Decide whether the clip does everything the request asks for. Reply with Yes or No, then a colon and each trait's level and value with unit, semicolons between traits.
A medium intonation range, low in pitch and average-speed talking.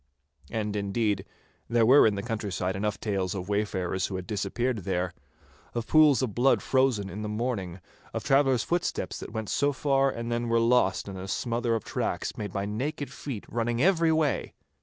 Yes: average, 4.4 semitones; low, 110 Hz; average, 185 wpm